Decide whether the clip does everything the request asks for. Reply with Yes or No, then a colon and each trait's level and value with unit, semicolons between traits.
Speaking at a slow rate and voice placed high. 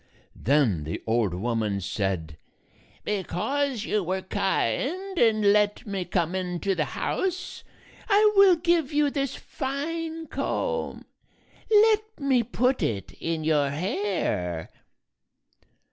Yes: slow, 115 wpm; high, 205 Hz